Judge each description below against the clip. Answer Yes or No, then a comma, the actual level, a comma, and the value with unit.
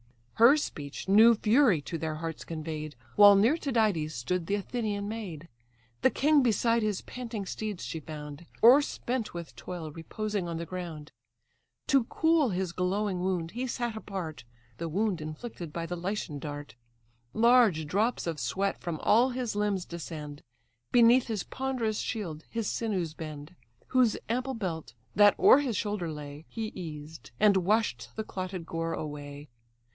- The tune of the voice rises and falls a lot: Yes, wide, 5.8 semitones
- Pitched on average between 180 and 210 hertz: Yes, high, 190 Hz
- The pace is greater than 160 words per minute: No, average, 155 wpm